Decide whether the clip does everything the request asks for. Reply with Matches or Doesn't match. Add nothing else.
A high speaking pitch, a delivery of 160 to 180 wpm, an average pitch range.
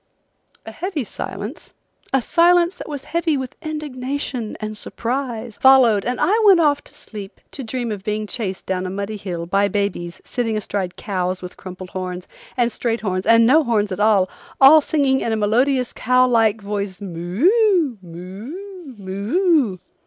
Doesn't match